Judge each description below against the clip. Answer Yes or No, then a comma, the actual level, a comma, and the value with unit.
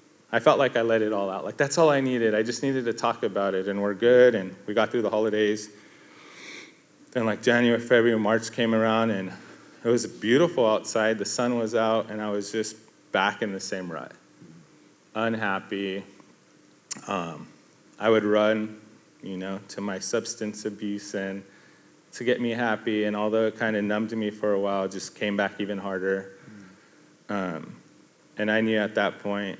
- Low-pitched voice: Yes, low, 105 Hz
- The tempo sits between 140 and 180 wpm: No, average, 190 wpm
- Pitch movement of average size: No, narrow, 2.2 semitones